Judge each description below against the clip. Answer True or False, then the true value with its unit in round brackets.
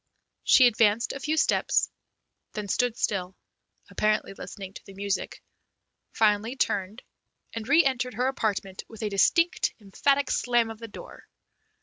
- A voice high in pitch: True (220 Hz)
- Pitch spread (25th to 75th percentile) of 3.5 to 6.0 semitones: True (3.8 semitones)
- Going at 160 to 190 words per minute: False (140 wpm)